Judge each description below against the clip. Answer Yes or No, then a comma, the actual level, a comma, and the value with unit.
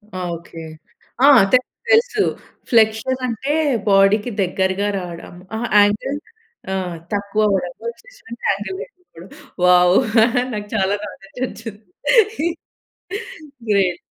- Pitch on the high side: Yes, high, 210 Hz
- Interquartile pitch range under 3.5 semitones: No, wide, 5.4 semitones